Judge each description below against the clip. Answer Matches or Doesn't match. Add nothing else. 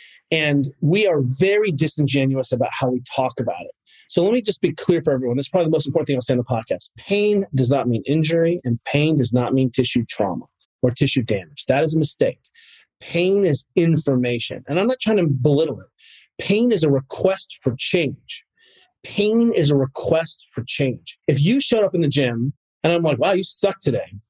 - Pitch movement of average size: Doesn't match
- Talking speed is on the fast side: Matches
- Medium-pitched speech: Matches